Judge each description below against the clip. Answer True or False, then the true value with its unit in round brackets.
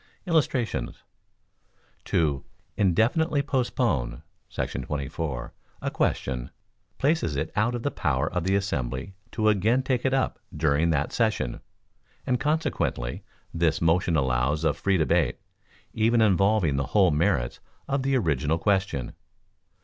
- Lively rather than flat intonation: True (8.3 semitones)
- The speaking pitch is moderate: False (90 Hz)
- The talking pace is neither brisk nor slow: False (125 wpm)